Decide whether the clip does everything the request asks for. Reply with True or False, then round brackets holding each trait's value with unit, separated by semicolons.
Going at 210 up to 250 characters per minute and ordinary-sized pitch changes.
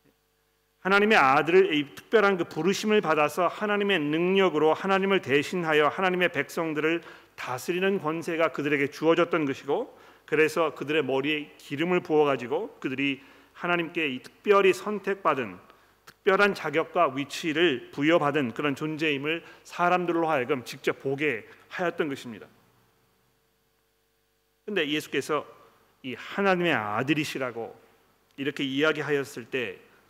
False (315 characters per minute; 4.1 semitones)